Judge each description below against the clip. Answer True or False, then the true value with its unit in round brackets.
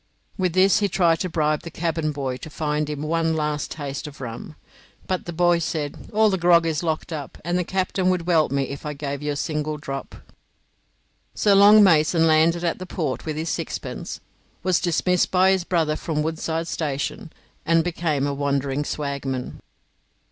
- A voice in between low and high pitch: True (160 Hz)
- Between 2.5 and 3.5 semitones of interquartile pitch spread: True (2.9 semitones)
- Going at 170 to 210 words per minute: True (190 wpm)